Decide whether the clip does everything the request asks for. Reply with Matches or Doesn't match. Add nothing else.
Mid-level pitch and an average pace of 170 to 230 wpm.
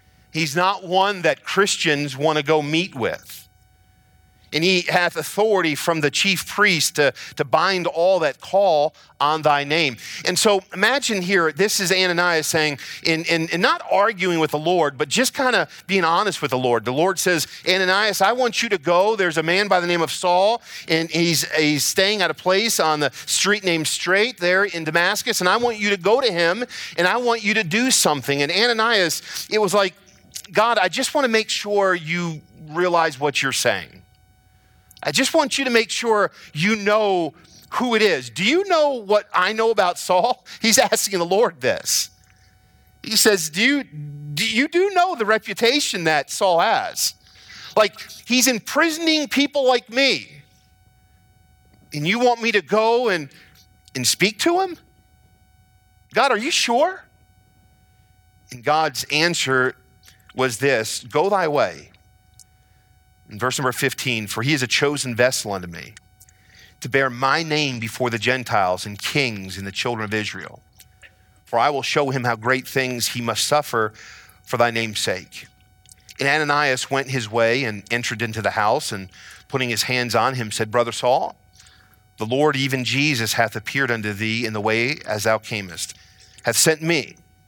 Matches